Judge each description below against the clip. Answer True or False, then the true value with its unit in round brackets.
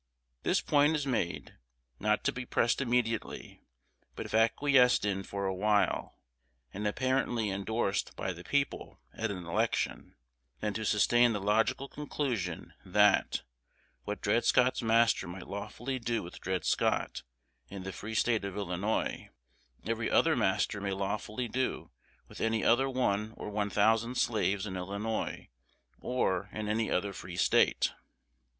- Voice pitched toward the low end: True (110 Hz)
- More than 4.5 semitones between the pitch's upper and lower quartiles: False (3.3 semitones)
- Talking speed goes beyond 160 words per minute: False (145 wpm)